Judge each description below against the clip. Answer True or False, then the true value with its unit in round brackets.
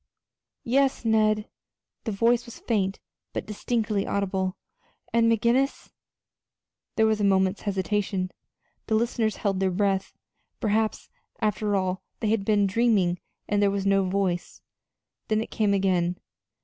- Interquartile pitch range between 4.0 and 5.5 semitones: False (2.4 semitones)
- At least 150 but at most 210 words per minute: False (135 wpm)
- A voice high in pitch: True (205 Hz)